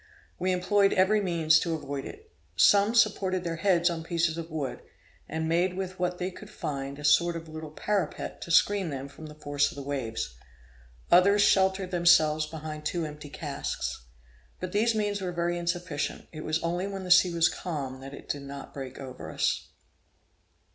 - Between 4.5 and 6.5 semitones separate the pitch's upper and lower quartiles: No, average, 3.7 semitones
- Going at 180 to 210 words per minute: Yes, average, 185 wpm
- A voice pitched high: No, medium, 170 Hz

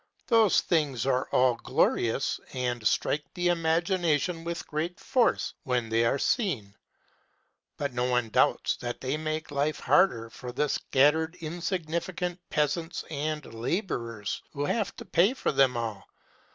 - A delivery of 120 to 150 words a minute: Yes, average, 140 wpm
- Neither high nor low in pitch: Yes, medium, 150 Hz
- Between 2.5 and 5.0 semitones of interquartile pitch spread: No, wide, 5.5 semitones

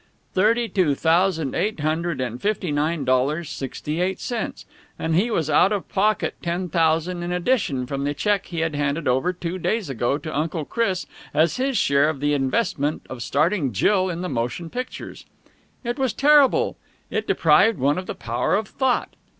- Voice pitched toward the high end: No, medium, 170 Hz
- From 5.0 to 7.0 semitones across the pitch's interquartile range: Yes, wide, 5.4 semitones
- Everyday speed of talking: Yes, average, 180 wpm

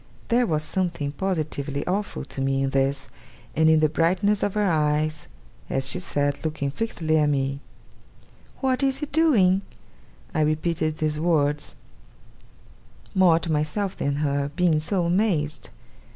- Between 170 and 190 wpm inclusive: No, average, 145 wpm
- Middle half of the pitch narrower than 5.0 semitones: Yes, average, 4.4 semitones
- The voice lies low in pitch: No, medium, 155 Hz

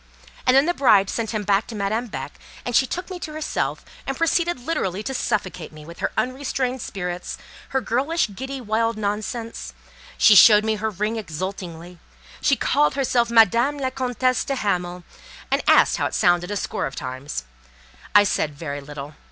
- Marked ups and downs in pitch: Yes, wide, 6.0 semitones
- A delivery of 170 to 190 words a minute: Yes, average, 175 wpm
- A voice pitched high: Yes, high, 220 Hz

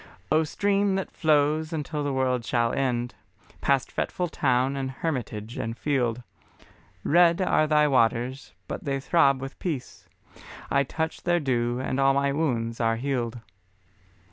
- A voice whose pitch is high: No, low, 135 Hz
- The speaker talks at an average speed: Yes, average, 145 wpm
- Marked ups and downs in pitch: No, average, 4.0 semitones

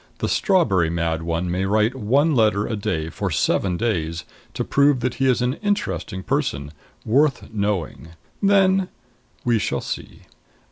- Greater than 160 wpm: No, average, 150 wpm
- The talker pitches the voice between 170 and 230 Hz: No, low, 105 Hz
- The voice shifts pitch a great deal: Yes, wide, 7.9 semitones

